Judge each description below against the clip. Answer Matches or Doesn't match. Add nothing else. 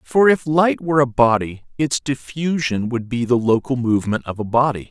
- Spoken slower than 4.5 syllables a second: Doesn't match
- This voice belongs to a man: Matches